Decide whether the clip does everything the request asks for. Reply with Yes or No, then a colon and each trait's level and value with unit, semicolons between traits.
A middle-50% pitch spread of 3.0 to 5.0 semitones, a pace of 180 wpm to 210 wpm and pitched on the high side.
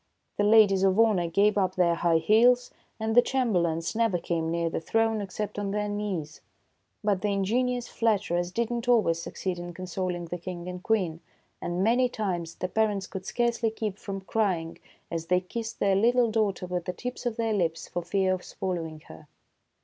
Yes: average, 4.1 semitones; average, 190 wpm; high, 195 Hz